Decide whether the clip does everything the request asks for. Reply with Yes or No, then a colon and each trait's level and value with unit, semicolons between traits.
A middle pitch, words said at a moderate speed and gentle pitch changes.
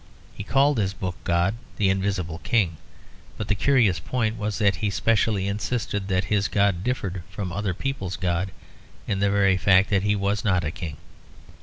No: low, 100 Hz; average, 180 wpm; narrow, 2.2 semitones